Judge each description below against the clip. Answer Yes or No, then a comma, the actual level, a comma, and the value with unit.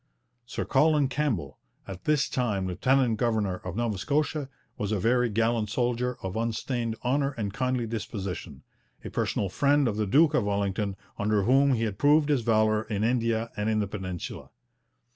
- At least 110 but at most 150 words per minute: No, average, 170 wpm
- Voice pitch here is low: Yes, low, 115 Hz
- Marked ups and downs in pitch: No, average, 4.0 semitones